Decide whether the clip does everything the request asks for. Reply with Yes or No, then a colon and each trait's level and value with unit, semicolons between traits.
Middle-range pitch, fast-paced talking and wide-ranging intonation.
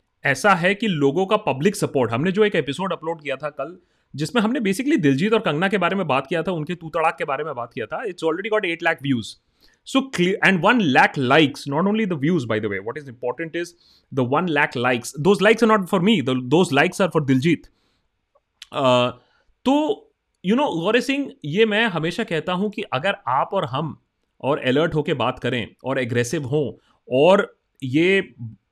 Yes: medium, 165 Hz; fast, 200 wpm; wide, 6.8 semitones